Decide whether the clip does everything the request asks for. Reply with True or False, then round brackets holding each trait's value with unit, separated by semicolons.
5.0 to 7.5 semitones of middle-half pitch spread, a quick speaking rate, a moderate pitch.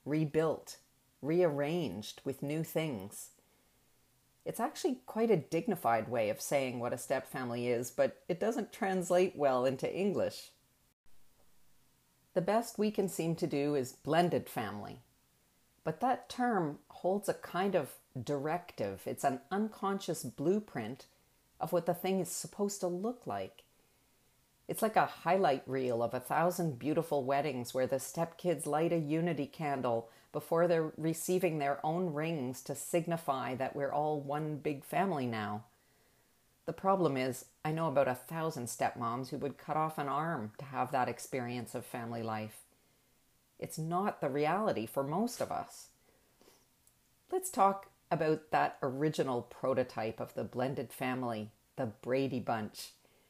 False (5.3 semitones; 145 wpm; 150 Hz)